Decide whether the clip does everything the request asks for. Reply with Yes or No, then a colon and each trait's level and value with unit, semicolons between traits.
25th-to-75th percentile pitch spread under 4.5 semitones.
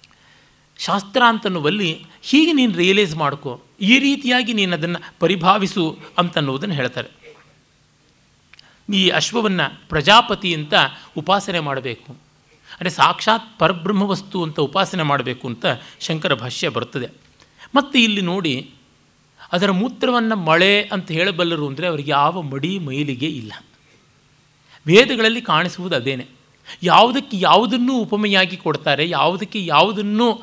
No: average, 5.3 semitones